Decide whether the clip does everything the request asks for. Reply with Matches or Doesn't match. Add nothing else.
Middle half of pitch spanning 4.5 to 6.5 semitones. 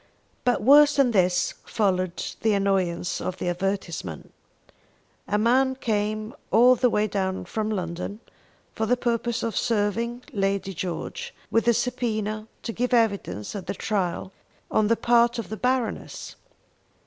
Doesn't match